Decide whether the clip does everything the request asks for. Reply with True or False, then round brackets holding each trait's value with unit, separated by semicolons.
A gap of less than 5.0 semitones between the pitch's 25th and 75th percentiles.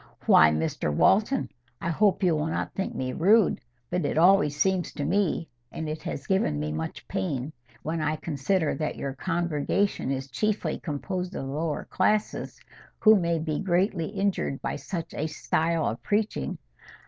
False (5.5 semitones)